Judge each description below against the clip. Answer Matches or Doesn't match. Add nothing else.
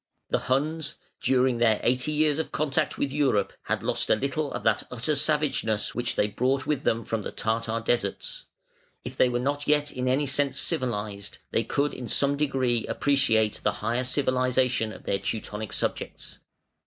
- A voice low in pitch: Matches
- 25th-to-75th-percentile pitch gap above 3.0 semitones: Matches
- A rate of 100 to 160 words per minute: Doesn't match